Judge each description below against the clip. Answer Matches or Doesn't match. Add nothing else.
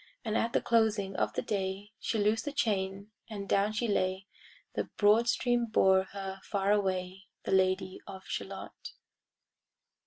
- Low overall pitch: Doesn't match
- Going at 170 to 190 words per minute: Doesn't match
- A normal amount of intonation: Doesn't match